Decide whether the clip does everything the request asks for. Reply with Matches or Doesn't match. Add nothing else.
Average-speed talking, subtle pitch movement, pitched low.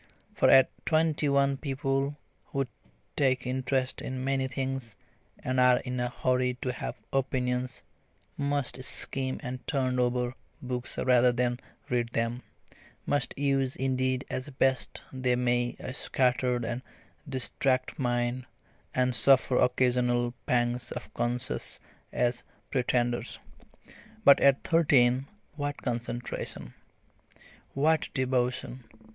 Doesn't match